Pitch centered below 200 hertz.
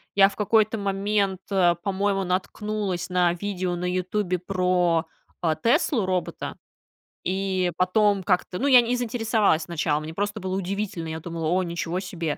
Yes: medium, 185 Hz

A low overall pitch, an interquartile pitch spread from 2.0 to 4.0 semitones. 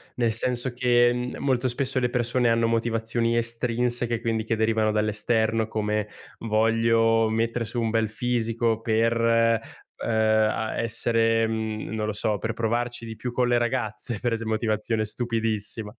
No: low, 115 Hz; narrow, 1.3 semitones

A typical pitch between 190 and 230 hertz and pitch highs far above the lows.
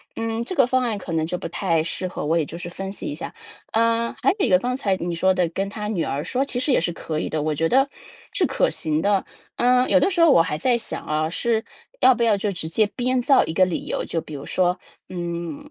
Yes: high, 195 Hz; wide, 6.6 semitones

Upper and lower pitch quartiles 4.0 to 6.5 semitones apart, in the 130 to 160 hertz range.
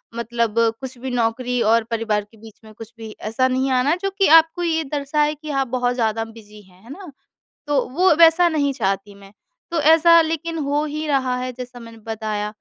No: average, 5.1 semitones; very high, 250 Hz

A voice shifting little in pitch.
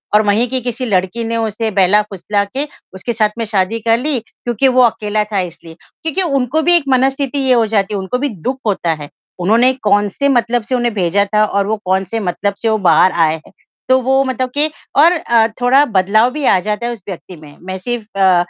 No: average, 4.3 semitones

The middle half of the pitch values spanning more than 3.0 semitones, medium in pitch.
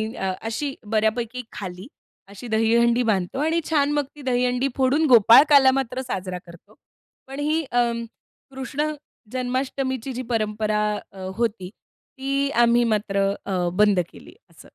No: average, 4.1 semitones; high, 245 Hz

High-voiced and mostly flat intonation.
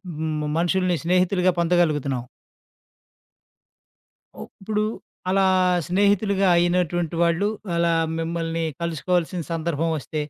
No: medium, 170 Hz; narrow, 1.9 semitones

